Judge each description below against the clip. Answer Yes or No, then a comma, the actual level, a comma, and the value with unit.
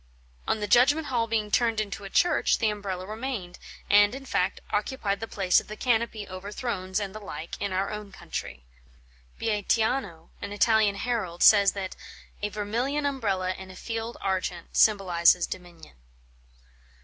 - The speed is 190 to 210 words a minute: No, average, 160 wpm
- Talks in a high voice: Yes, high, 205 Hz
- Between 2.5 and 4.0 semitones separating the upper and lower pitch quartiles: Yes, average, 3.3 semitones